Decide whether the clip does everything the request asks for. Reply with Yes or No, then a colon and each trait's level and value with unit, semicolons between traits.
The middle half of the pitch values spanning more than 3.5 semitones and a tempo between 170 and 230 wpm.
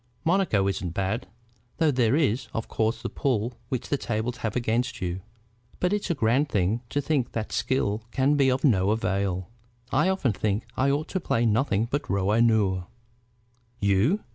Yes: average, 5.2 semitones; average, 185 wpm